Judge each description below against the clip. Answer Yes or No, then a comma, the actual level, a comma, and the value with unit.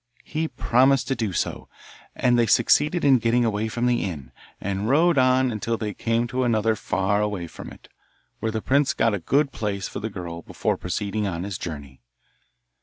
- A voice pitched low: Yes, low, 110 Hz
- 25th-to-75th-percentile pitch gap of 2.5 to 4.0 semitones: No, average, 4.4 semitones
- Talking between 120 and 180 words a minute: No, average, 190 wpm